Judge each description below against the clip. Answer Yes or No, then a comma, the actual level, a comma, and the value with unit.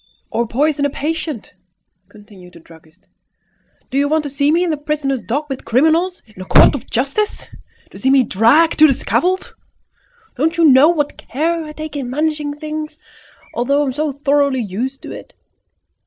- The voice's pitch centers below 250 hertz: No, very high, 285 Hz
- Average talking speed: Yes, average, 185 wpm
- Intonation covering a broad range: No, average, 3.5 semitones